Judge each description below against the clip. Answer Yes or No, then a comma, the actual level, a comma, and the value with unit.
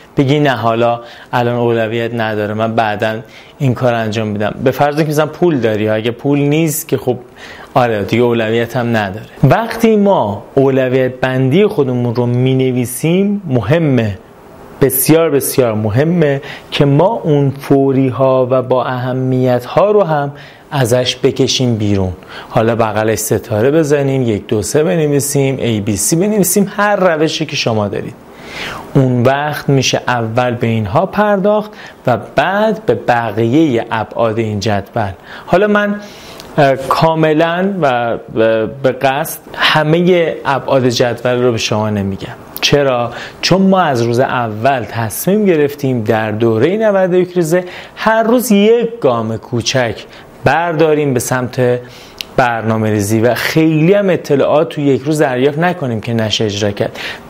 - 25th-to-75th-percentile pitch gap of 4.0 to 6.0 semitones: Yes, average, 5.2 semitones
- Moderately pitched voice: No, low, 130 Hz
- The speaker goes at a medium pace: Yes, average, 140 wpm